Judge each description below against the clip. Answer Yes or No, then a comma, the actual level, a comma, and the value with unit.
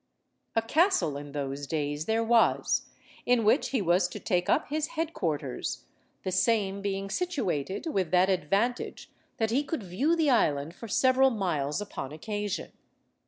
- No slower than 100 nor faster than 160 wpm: Yes, average, 155 wpm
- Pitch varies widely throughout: Yes, wide, 7.1 semitones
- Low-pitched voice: No, high, 200 Hz